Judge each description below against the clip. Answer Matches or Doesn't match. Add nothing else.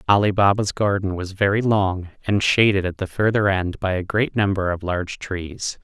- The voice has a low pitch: Matches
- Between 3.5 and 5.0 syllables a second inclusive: Matches